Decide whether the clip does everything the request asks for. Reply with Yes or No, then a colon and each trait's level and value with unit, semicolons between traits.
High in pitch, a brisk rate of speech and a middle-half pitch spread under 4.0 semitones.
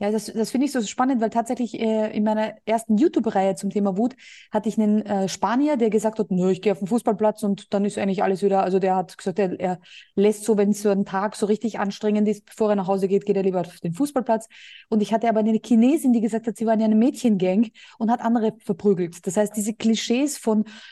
Yes: high, 215 Hz; fast, 250 wpm; narrow, 2.4 semitones